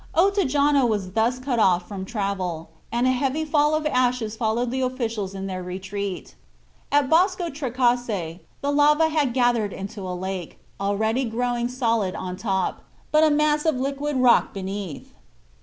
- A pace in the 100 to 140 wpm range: No, average, 155 wpm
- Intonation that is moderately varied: No, wide, 6.2 semitones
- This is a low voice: No, high, 240 Hz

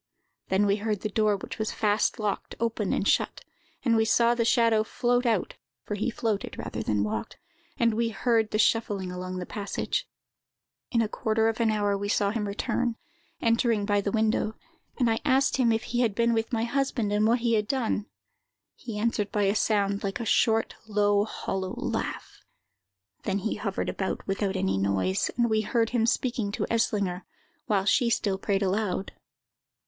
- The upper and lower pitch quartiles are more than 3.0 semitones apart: No, narrow, 2.4 semitones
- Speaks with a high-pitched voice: Yes, high, 215 Hz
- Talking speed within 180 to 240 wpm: Yes, average, 185 wpm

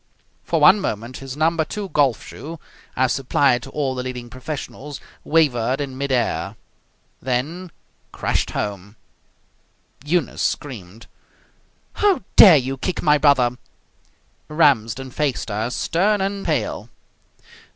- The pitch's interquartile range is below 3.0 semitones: No, average, 4.4 semitones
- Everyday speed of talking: No, slow, 120 wpm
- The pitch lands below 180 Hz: Yes, low, 135 Hz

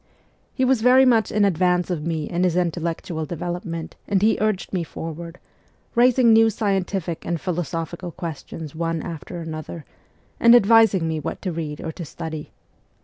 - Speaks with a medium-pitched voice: Yes, medium, 175 Hz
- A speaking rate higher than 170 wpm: No, average, 160 wpm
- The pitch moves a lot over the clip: No, average, 3.8 semitones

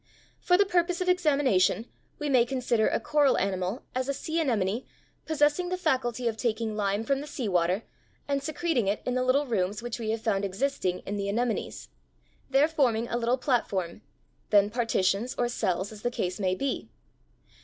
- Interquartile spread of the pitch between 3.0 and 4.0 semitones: No, average, 5.3 semitones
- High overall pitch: Yes, high, 240 Hz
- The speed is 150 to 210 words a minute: Yes, average, 190 wpm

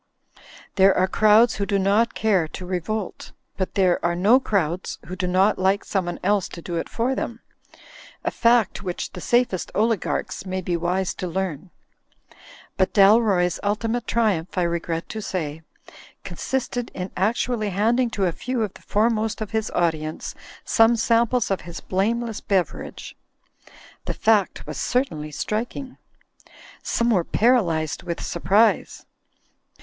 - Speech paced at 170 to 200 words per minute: No, average, 150 wpm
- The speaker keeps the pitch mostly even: No, average, 4.0 semitones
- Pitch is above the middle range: Yes, high, 200 Hz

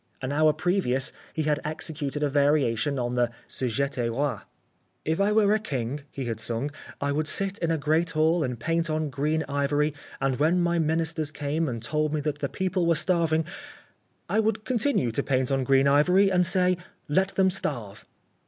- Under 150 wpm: No, average, 190 wpm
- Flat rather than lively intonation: No, average, 3.7 semitones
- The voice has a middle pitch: Yes, medium, 150 Hz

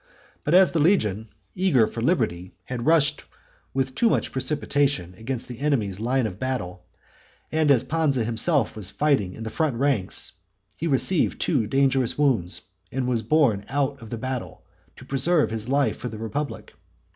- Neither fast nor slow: Yes, average, 170 wpm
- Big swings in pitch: No, average, 4.6 semitones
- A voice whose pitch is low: Yes, low, 130 Hz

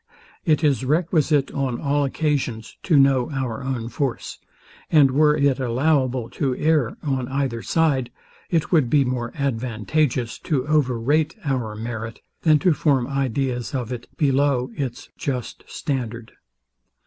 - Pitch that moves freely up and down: No, average, 3.2 semitones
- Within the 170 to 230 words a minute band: No, average, 140 wpm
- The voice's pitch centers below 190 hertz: Yes, low, 135 Hz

